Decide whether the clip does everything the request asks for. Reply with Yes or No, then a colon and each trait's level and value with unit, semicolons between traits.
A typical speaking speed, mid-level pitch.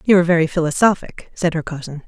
Yes: average, 175 wpm; medium, 170 Hz